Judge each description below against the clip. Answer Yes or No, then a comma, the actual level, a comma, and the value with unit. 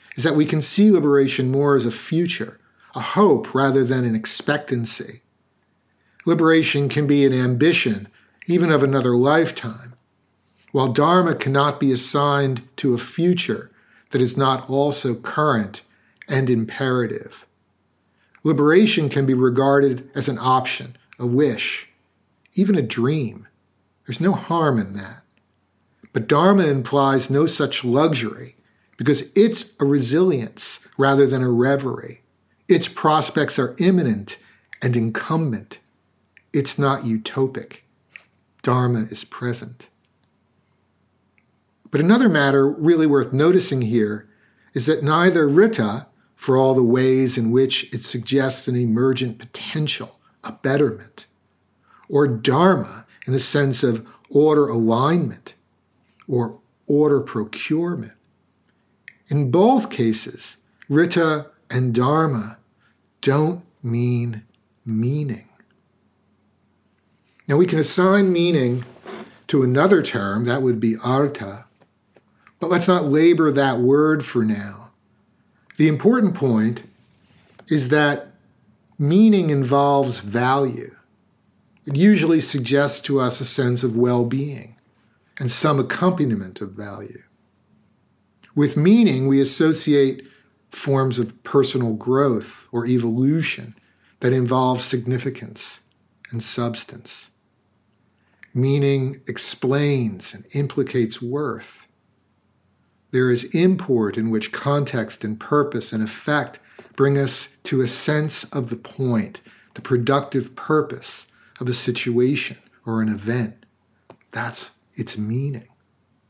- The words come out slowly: Yes, slow, 115 wpm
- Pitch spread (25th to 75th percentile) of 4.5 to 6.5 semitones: No, average, 3.8 semitones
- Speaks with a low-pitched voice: Yes, low, 130 Hz